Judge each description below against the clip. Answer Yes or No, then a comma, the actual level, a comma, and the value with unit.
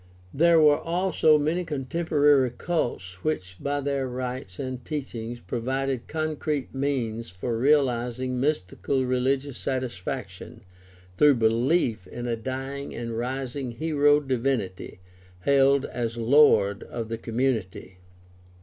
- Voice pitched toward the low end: Yes, low, 130 Hz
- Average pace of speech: No, slow, 115 wpm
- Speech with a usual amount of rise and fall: Yes, average, 3.6 semitones